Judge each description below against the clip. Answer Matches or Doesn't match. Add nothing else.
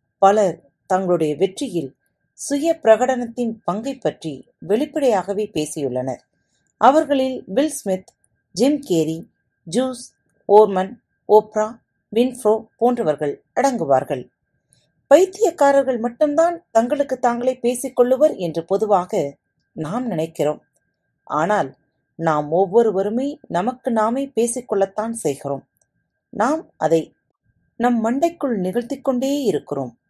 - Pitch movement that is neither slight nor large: Doesn't match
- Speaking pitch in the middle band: Doesn't match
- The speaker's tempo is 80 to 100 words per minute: Matches